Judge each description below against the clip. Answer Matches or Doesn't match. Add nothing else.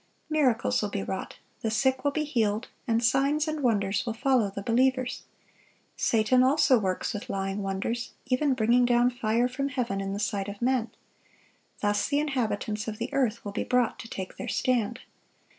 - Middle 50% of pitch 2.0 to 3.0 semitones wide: Doesn't match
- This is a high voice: Matches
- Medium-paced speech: Matches